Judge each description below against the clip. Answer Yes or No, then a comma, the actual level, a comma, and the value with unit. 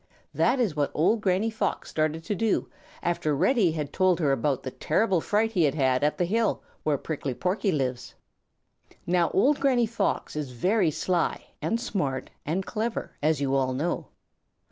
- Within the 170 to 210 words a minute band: Yes, average, 175 wpm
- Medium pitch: Yes, medium, 175 Hz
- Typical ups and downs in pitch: No, wide, 6.6 semitones